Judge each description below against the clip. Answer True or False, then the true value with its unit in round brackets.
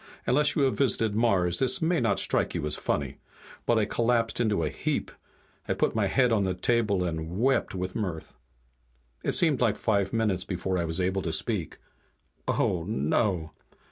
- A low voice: True (100 Hz)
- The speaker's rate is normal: True (180 wpm)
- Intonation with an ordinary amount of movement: True (4.7 semitones)